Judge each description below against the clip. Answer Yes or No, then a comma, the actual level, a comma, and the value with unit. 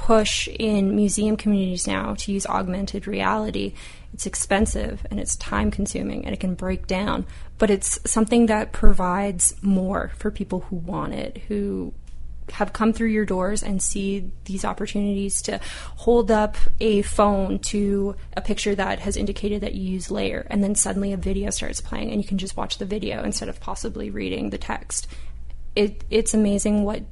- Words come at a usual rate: Yes, average, 175 wpm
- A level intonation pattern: Yes, narrow, 2.1 semitones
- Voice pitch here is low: No, high, 200 Hz